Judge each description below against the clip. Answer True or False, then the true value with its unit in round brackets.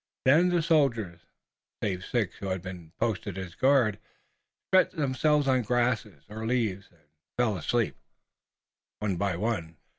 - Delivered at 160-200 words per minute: False (140 wpm)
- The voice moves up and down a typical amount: False (5.7 semitones)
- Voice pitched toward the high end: False (110 Hz)